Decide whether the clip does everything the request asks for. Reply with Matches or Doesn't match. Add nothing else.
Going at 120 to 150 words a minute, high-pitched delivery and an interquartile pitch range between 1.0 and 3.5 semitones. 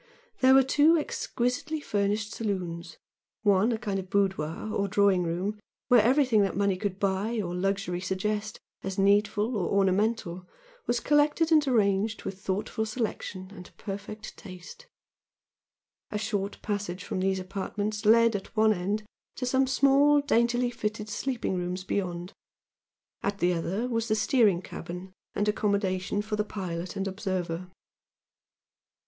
Matches